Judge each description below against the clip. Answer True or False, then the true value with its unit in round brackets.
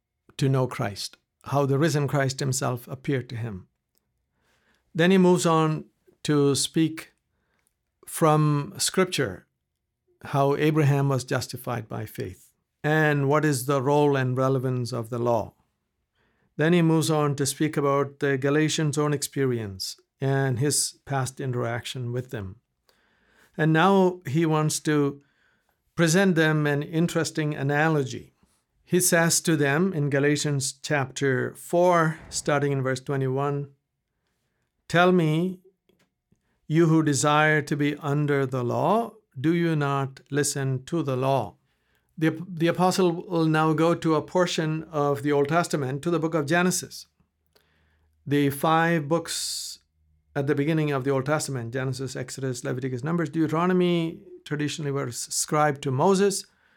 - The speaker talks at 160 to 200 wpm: False (135 wpm)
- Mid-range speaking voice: True (145 Hz)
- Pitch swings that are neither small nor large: True (3.3 semitones)